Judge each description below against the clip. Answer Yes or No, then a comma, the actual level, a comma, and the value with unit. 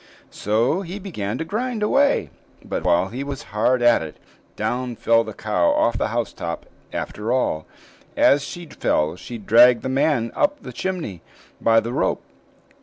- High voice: No, low, 120 Hz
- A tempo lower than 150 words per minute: No, average, 170 wpm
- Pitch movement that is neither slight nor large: No, wide, 6.7 semitones